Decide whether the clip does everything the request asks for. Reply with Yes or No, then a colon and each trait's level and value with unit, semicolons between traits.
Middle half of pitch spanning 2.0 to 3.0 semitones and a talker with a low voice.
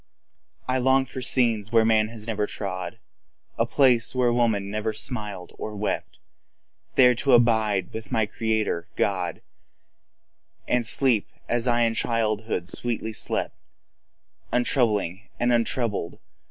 Yes: narrow, 2.5 semitones; low, 115 Hz